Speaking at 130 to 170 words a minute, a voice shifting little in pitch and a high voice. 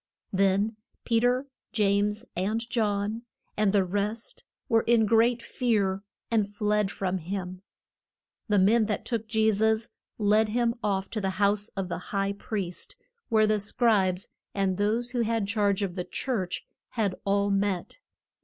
Yes: average, 155 wpm; narrow, 2.3 semitones; high, 210 Hz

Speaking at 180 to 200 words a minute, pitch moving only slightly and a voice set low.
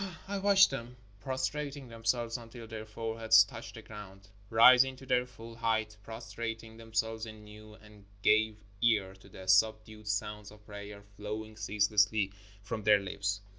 No: average, 150 wpm; narrow, 1.6 semitones; low, 110 Hz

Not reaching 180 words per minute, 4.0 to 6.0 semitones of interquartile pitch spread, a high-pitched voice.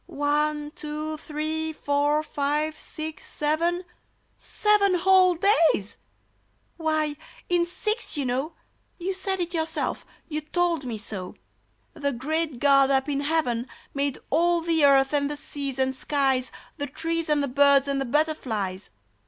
No: average, 150 wpm; average, 2.9 semitones; very high, 300 Hz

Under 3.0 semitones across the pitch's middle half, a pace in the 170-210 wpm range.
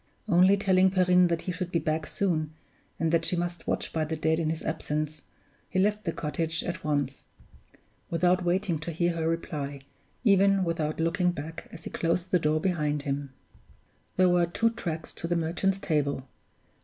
Yes: narrow, 2.6 semitones; average, 180 wpm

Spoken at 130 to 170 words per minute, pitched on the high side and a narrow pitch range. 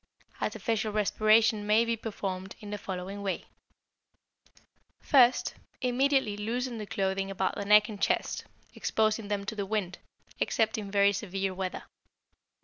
Yes: average, 140 wpm; high, 210 Hz; narrow, 2.2 semitones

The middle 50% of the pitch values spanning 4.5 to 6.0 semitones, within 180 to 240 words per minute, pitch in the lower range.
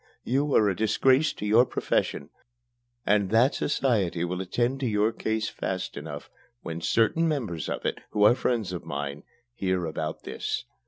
No: wide, 5.6 semitones; average, 165 wpm; low, 105 Hz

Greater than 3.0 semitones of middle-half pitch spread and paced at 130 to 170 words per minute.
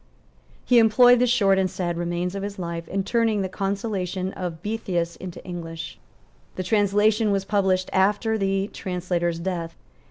No: average, 2.7 semitones; average, 155 wpm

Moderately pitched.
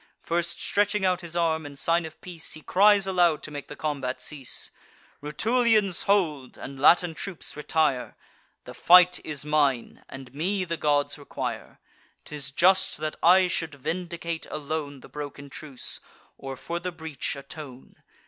Yes: medium, 160 Hz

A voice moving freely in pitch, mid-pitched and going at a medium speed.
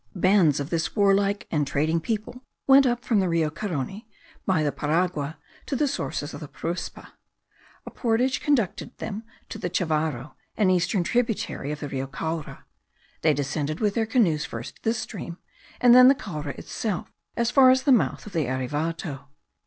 Yes: wide, 6.7 semitones; medium, 180 Hz; average, 175 wpm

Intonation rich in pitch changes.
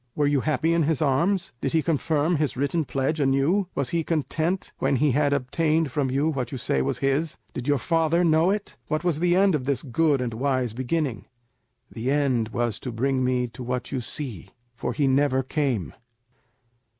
No: average, 3.8 semitones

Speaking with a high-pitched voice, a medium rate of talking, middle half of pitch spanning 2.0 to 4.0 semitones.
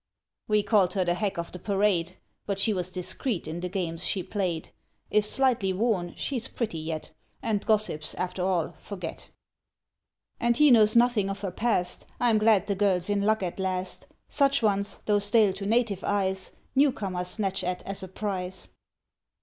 Yes: high, 195 Hz; average, 175 wpm; average, 2.9 semitones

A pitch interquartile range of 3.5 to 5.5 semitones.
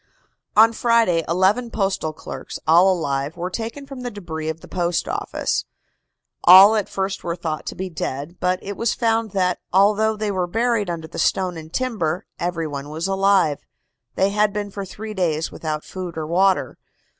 Yes: average, 4.1 semitones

